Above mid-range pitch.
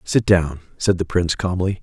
No: very low, 90 Hz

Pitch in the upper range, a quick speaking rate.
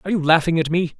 No: medium, 165 Hz; fast, 305 wpm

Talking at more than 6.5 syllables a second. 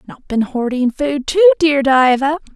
No: 4.4 syllables/s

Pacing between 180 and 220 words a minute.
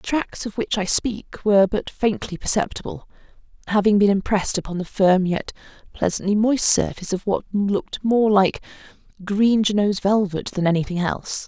No: average, 155 wpm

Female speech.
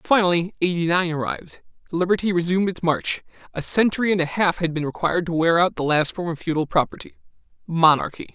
No: male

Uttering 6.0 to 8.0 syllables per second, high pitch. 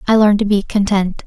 No: 5.6 syllables/s; high, 205 Hz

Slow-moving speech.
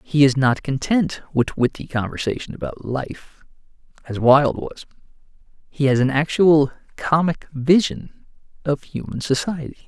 Yes: slow, 130 wpm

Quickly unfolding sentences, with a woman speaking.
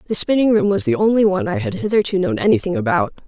Yes: fast, 240 wpm; female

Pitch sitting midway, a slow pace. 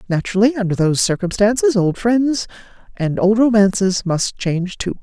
No: high, 205 Hz; slow, 120 wpm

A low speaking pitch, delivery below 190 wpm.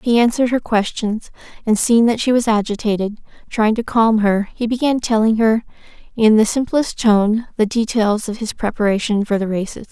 No: high, 220 Hz; average, 180 wpm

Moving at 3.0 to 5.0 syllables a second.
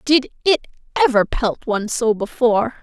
Yes: 4.9 syllables/s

